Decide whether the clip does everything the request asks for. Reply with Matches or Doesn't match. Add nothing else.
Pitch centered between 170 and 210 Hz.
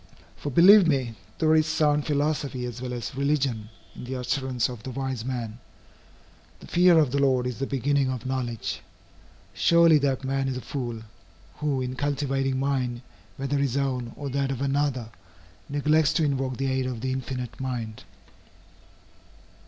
Doesn't match